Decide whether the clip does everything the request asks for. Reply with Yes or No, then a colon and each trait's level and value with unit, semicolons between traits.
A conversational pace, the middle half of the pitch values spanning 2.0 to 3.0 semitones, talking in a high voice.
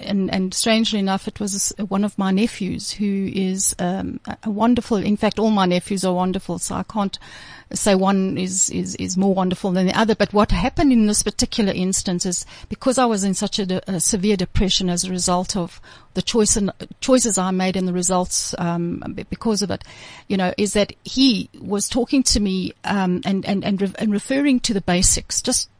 No: fast, 210 wpm; narrow, 2.4 semitones; high, 195 Hz